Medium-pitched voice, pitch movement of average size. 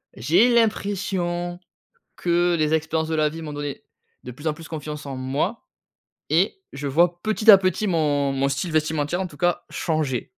Yes: medium, 160 Hz; average, 3.3 semitones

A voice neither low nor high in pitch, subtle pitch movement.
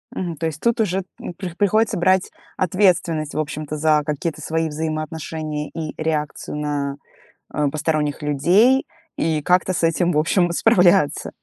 No: medium, 160 Hz; average, 3.0 semitones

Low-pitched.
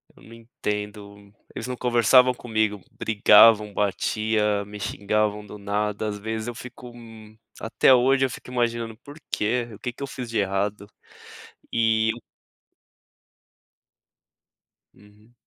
Yes: low, 110 Hz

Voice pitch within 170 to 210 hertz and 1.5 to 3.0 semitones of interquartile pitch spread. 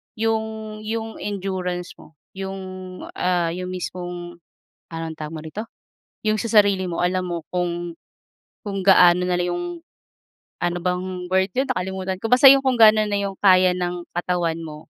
Yes: medium, 185 Hz; average, 2.7 semitones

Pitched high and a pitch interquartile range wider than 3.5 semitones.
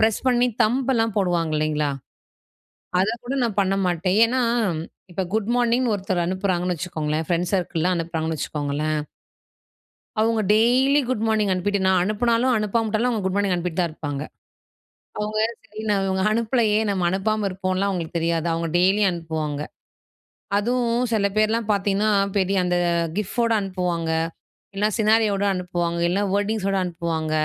Yes: high, 195 Hz; average, 4.0 semitones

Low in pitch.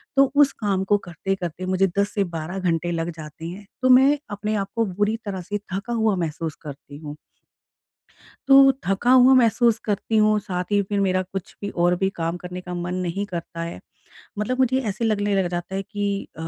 No: high, 195 Hz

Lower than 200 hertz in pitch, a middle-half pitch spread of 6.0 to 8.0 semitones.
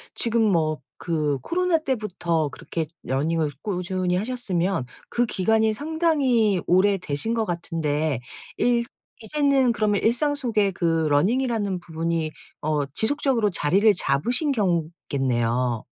Yes: medium, 185 Hz; wide, 6.9 semitones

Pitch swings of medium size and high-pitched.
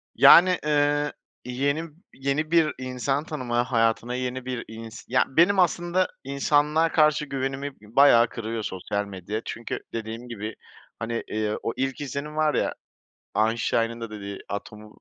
No: average, 4.5 semitones; low, 130 Hz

